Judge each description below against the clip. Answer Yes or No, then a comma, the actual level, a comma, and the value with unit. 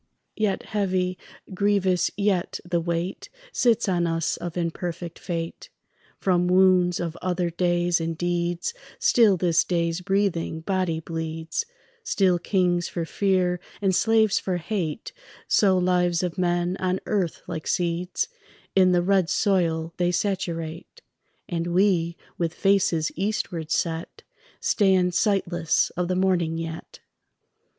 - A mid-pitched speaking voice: Yes, medium, 180 Hz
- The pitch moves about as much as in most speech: No, narrow, 2.1 semitones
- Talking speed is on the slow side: Yes, slow, 125 wpm